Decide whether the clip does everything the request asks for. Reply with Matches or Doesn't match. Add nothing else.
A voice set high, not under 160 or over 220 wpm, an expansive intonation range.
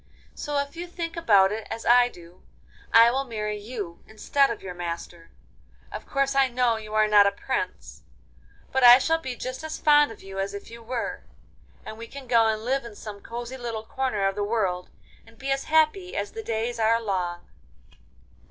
Doesn't match